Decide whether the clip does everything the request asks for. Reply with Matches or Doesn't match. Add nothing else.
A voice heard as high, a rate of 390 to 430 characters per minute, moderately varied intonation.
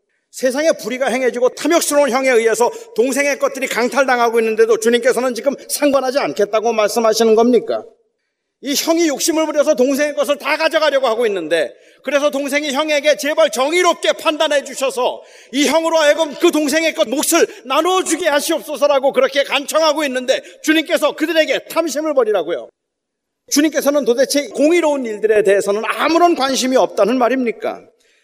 Matches